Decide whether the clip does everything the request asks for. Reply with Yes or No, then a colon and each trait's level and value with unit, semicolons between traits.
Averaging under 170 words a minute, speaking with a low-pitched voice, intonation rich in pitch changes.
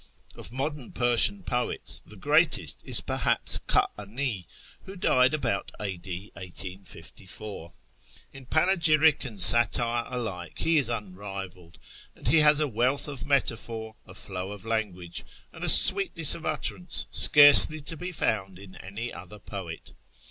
Yes: slow, 135 wpm; low, 115 Hz; wide, 7.1 semitones